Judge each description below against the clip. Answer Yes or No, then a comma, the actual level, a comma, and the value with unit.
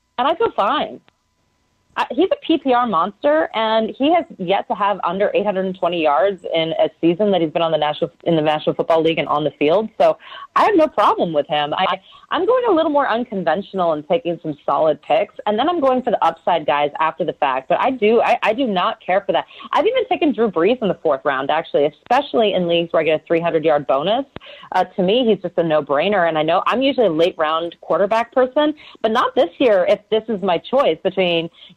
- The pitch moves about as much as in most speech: No, wide, 7.6 semitones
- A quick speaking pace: Yes, fast, 235 wpm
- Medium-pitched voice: No, high, 195 Hz